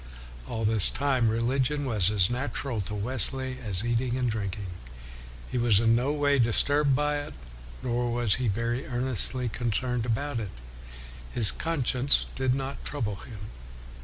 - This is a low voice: Yes, low, 120 Hz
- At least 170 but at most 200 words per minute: No, average, 155 wpm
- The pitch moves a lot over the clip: No, average, 3.0 semitones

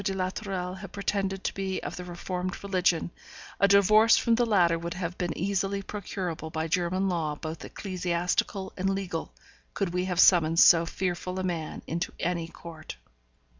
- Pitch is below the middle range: No, medium, 180 Hz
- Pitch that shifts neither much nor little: No, narrow, 2.2 semitones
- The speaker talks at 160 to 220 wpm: Yes, average, 170 wpm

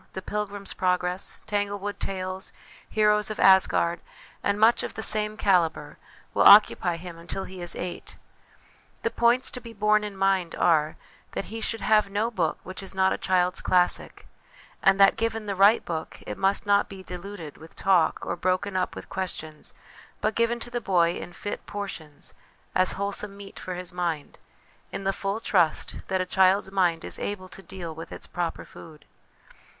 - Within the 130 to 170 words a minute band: No, average, 180 wpm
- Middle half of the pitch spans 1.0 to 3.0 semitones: Yes, narrow, 2.5 semitones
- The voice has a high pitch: Yes, high, 195 Hz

